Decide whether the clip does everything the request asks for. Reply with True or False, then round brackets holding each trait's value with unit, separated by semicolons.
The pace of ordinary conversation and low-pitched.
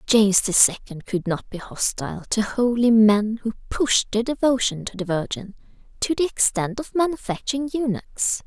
False (165 wpm; 225 Hz)